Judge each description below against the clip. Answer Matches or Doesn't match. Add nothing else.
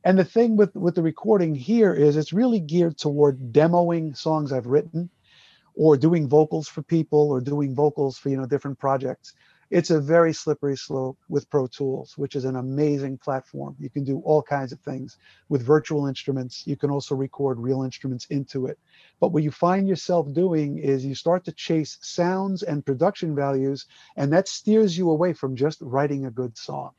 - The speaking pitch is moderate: Matches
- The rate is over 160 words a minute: Matches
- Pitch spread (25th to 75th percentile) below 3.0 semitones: Doesn't match